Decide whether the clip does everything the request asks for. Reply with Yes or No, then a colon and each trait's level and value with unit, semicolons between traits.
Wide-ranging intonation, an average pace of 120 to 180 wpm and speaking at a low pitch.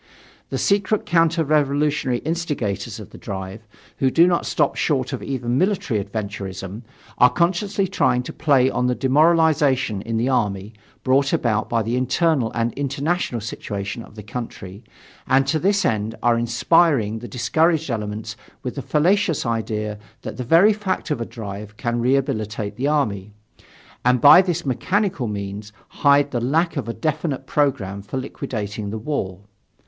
Yes: wide, 6.0 semitones; average, 160 wpm; low, 130 Hz